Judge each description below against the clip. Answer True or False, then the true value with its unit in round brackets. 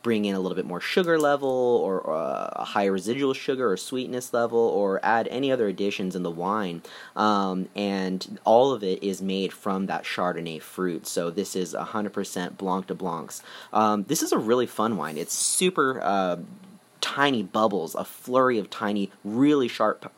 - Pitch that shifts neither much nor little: True (5.0 semitones)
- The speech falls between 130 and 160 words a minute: False (180 wpm)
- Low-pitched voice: True (100 Hz)